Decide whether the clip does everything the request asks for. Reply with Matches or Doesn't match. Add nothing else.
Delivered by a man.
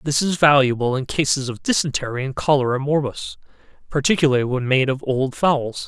Matches